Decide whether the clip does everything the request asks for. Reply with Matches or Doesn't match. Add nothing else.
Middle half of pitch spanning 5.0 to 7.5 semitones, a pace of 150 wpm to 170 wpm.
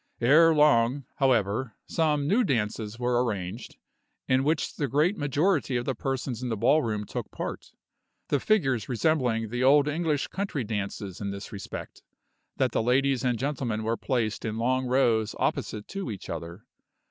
Doesn't match